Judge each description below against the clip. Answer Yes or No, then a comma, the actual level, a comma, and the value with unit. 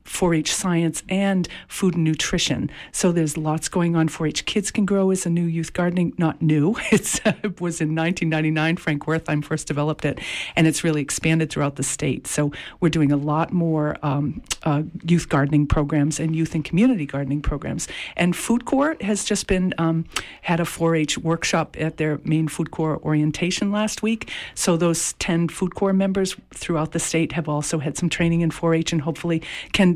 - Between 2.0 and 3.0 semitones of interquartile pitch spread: Yes, narrow, 2.5 semitones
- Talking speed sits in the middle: Yes, average, 190 wpm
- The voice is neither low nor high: Yes, medium, 165 Hz